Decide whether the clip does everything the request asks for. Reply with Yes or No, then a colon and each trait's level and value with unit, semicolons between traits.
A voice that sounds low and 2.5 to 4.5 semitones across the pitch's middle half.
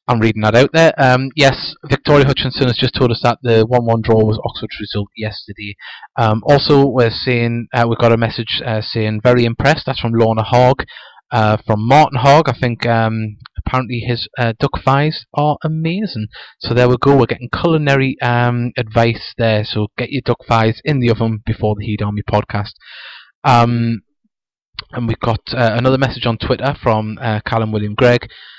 Yes: low, 120 Hz; average, 3.1 semitones